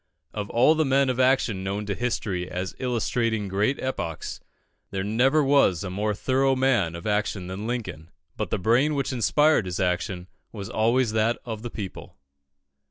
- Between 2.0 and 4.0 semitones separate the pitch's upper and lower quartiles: No, average, 5.2 semitones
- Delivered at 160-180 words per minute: Yes, average, 170 wpm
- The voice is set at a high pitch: No, low, 110 Hz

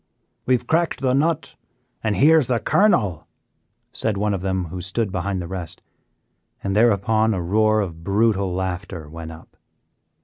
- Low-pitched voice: Yes, low, 100 Hz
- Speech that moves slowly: No, average, 165 wpm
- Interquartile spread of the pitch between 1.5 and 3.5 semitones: No, average, 4.0 semitones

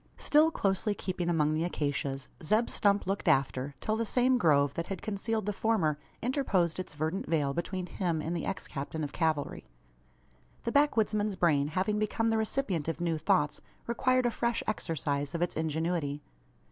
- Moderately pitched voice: Yes, medium, 175 Hz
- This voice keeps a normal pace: Yes, average, 170 wpm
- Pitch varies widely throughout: Yes, wide, 5.8 semitones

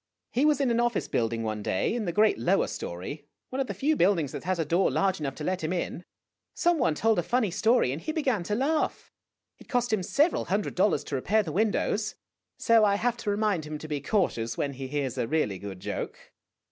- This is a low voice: No, high, 190 Hz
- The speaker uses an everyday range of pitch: No, wide, 7.8 semitones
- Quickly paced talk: Yes, fast, 235 wpm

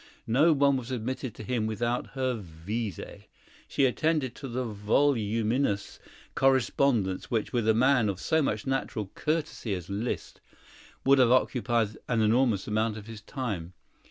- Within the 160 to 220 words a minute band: No, average, 150 wpm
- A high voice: No, low, 115 Hz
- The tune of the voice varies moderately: Yes, average, 3.8 semitones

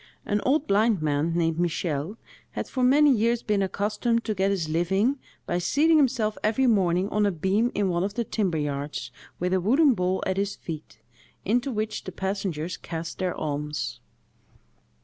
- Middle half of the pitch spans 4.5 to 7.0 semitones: Yes, average, 4.8 semitones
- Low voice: No, high, 195 Hz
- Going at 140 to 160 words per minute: No, average, 175 wpm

